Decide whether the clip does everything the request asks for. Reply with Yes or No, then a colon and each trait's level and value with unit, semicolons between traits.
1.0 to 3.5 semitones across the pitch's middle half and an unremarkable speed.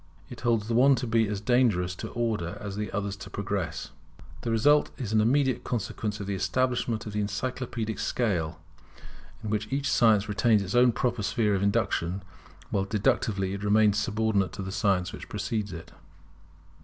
Yes: average, 3.0 semitones; average, 180 wpm